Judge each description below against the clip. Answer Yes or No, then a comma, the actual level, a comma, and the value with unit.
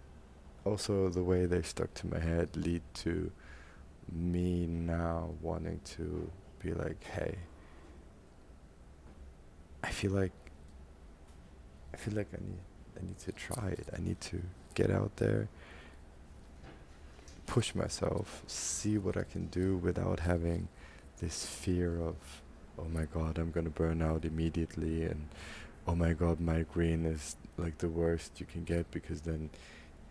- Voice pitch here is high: No, very low, 80 Hz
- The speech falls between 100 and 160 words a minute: Yes, average, 140 wpm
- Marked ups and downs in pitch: No, average, 3.0 semitones